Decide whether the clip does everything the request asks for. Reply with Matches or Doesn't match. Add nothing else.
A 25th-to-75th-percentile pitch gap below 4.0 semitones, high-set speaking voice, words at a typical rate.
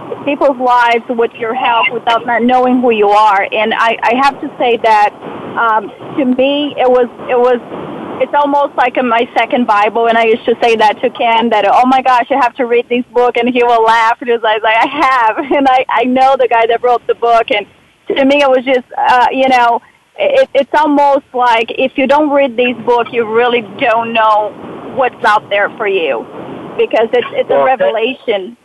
Doesn't match